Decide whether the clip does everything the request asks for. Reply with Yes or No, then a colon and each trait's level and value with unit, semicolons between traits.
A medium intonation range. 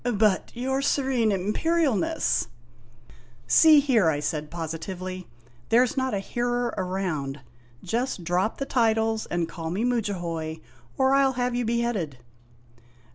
No: wide, 6.6 semitones